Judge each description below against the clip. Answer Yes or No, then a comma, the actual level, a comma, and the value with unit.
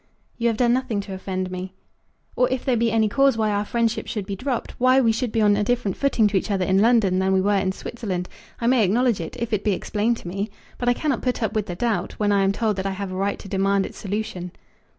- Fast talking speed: Yes, fast, 270 wpm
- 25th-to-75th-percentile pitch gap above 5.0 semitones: No, average, 3.5 semitones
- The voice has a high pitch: Yes, high, 210 Hz